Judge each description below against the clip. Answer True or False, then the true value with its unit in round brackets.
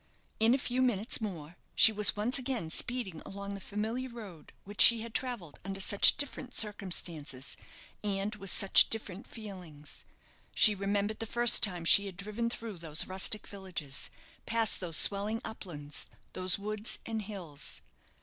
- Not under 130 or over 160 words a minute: True (155 wpm)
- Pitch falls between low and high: False (200 Hz)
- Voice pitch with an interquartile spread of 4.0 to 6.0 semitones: False (3.4 semitones)